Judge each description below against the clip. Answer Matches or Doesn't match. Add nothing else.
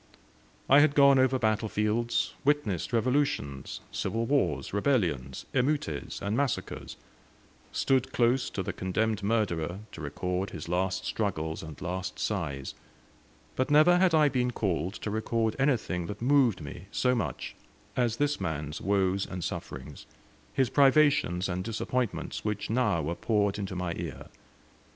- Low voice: Matches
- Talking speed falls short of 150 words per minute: Matches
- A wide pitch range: Matches